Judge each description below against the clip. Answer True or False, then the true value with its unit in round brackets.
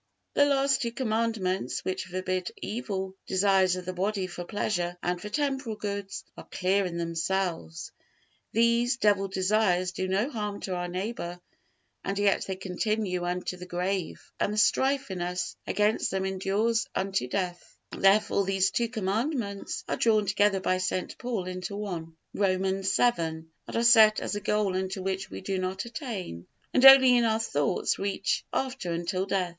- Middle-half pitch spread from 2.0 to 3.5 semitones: True (2.9 semitones)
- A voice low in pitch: False (195 Hz)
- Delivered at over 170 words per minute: False (165 wpm)